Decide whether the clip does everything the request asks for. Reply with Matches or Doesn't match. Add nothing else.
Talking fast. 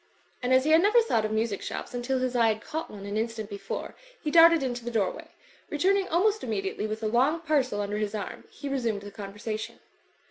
Matches